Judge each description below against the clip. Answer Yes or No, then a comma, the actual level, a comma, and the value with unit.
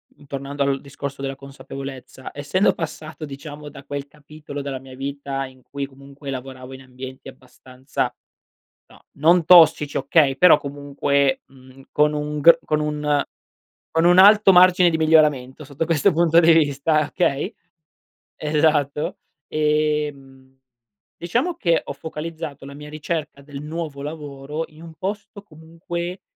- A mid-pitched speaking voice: Yes, medium, 150 Hz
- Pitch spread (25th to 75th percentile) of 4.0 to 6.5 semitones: No, average, 2.7 semitones